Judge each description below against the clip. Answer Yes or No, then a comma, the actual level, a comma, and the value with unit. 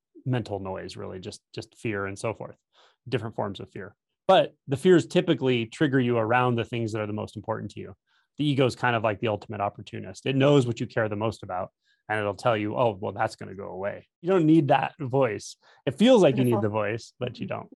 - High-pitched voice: No, low, 115 Hz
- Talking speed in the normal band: No, fast, 245 wpm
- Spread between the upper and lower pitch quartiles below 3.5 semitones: No, average, 4.2 semitones